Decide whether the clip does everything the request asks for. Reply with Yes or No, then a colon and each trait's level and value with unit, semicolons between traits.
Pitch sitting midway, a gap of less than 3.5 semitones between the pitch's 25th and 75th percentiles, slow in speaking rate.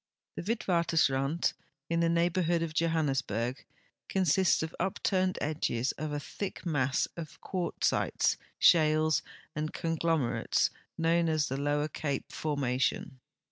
Yes: medium, 160 Hz; average, 2.8 semitones; slow, 115 wpm